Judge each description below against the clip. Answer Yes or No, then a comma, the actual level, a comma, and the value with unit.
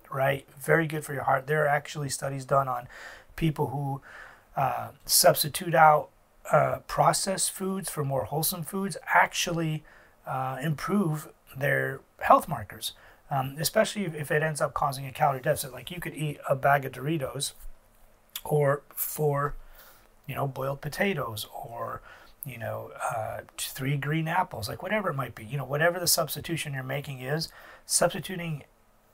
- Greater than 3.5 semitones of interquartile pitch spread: No, average, 3.2 semitones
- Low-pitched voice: No, medium, 150 Hz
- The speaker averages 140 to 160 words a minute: Yes, average, 155 wpm